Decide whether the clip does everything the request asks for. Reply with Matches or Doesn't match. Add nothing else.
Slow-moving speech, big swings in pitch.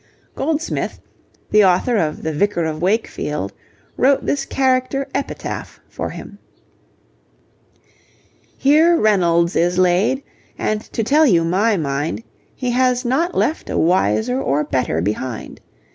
Matches